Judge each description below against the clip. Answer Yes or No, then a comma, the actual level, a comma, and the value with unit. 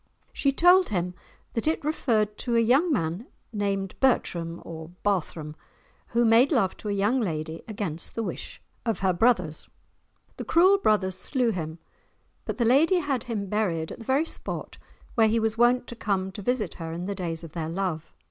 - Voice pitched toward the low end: No, high, 210 Hz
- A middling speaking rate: Yes, average, 185 wpm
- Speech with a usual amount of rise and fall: No, wide, 5.8 semitones